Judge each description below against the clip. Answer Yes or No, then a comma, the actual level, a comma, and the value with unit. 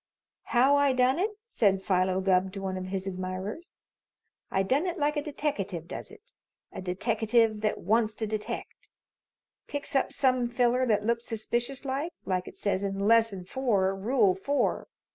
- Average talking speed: Yes, average, 165 wpm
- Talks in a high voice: Yes, high, 220 Hz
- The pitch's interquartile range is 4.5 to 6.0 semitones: Yes, wide, 5.6 semitones